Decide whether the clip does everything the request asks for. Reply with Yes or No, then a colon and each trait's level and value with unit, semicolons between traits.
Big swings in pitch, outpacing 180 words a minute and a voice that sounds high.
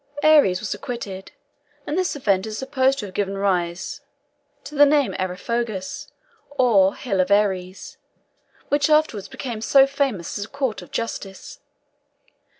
No: wide, 6.3 semitones; average, 145 wpm; high, 220 Hz